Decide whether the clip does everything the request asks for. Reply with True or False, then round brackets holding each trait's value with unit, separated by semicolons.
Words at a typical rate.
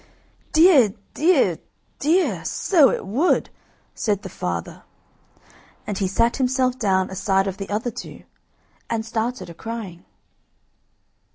False (120 wpm)